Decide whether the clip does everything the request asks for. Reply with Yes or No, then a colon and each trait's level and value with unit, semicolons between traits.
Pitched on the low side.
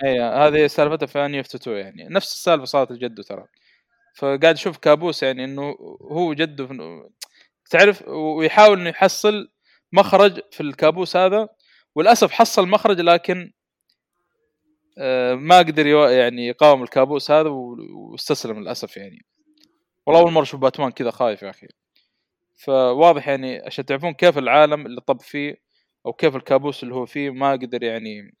No: medium, 150 Hz